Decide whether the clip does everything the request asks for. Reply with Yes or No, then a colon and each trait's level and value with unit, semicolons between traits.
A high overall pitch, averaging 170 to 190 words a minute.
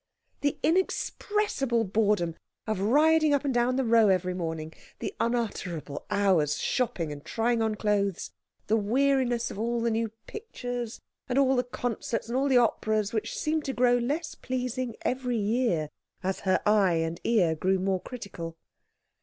No: high, 230 Hz; average, 160 wpm